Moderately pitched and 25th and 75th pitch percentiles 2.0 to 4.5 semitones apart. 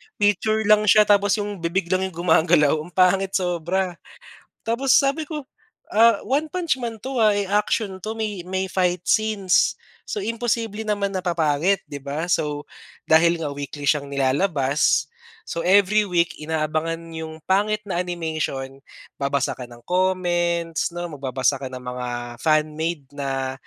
No: medium, 180 Hz; average, 5.3 semitones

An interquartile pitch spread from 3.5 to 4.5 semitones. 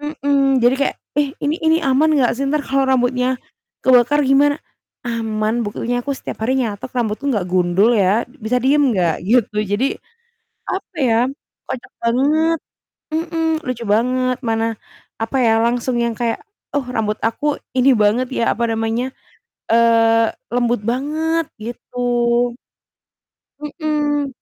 Yes: average, 3.9 semitones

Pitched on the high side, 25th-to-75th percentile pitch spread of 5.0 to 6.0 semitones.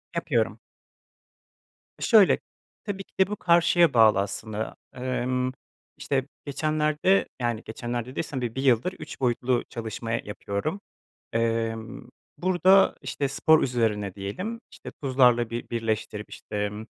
No: low, 125 Hz; wide, 5.5 semitones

